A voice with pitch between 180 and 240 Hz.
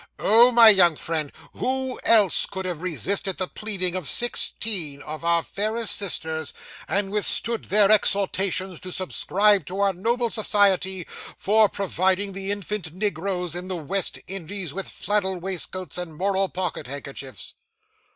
Yes: high, 190 Hz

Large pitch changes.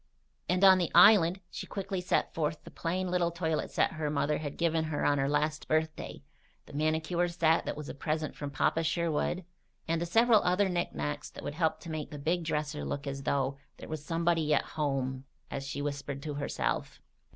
No: average, 2.8 semitones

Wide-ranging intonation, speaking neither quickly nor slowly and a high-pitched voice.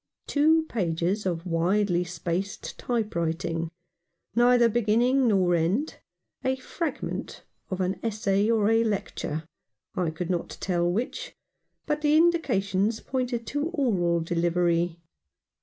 No: wide, 5.8 semitones; slow, 130 wpm; high, 200 Hz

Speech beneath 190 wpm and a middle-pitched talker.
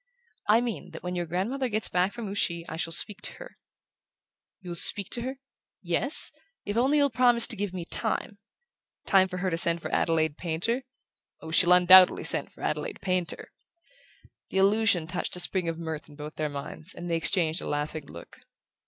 No: average, 195 wpm; medium, 180 Hz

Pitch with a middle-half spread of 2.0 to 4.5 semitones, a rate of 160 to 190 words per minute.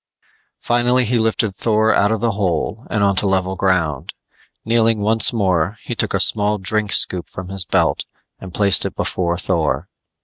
Yes: average, 3.0 semitones; average, 170 wpm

